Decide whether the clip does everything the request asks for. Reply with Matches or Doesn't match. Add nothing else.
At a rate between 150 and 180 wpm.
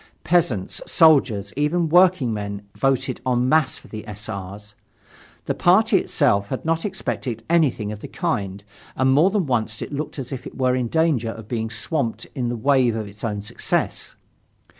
Matches